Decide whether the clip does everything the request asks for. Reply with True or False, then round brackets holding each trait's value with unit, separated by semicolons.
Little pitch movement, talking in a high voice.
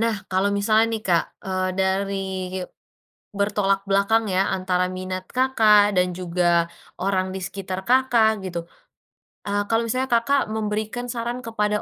False (3.3 semitones; 200 Hz)